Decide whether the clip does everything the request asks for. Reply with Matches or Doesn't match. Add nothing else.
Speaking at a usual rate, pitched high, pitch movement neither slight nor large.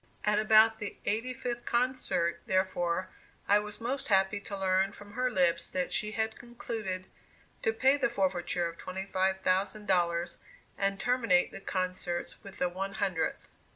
Matches